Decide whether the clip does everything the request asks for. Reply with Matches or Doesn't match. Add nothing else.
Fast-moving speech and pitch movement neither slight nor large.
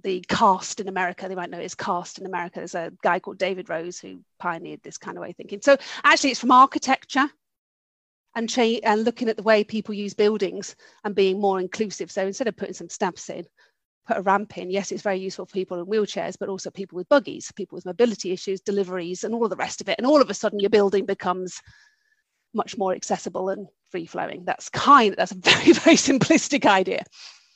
Matches